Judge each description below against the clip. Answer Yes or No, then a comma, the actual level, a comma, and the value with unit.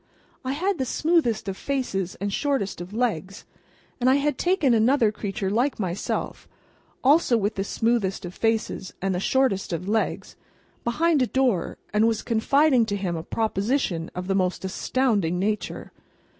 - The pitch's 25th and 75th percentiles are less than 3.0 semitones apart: No, average, 5.3 semitones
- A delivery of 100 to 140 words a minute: No, average, 165 wpm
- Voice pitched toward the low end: No, high, 220 Hz